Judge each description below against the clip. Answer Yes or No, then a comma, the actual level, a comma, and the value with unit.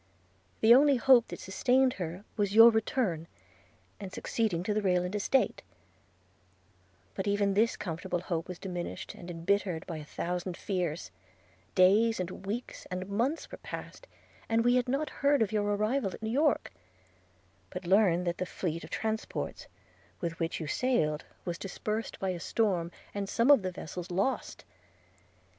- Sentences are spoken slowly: No, average, 165 wpm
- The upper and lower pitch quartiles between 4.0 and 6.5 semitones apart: Yes, average, 4.4 semitones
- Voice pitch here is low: No, high, 195 Hz